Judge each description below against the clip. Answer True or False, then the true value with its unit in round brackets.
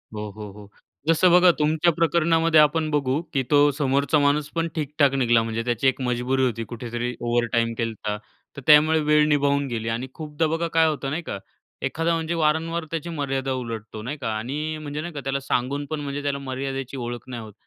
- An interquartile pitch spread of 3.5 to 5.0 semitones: True (4.2 semitones)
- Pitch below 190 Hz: True (140 Hz)